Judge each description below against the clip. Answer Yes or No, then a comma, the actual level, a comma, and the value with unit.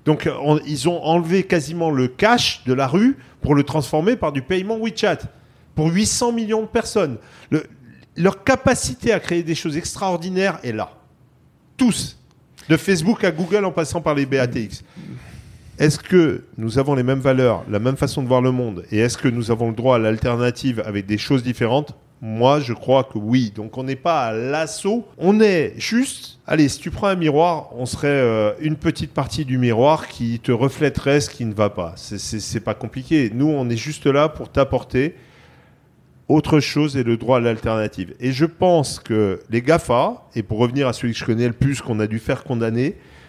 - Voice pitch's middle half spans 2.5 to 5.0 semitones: No, wide, 5.4 semitones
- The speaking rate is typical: Yes, average, 200 wpm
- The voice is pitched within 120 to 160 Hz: Yes, medium, 140 Hz